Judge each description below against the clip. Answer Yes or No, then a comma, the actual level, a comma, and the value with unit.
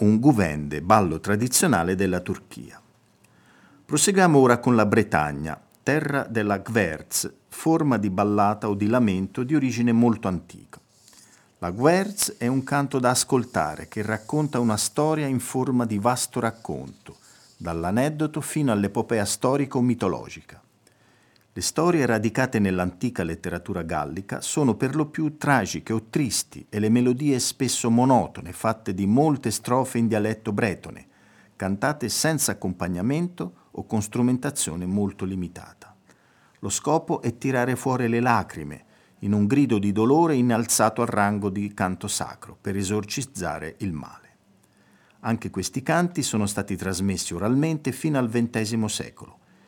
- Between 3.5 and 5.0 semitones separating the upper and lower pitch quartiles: Yes, average, 4.5 semitones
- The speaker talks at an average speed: Yes, average, 135 wpm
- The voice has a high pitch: No, low, 115 Hz